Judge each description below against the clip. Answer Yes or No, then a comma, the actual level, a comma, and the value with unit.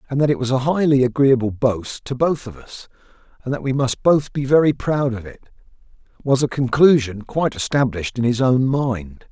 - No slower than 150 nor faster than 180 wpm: No, average, 200 wpm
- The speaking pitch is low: Yes, low, 130 Hz